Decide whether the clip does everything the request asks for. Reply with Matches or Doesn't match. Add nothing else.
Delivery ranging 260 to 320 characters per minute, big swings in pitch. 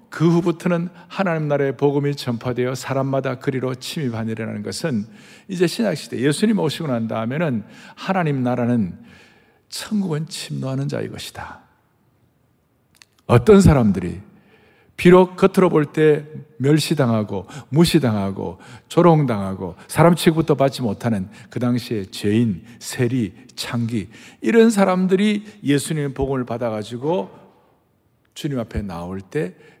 Matches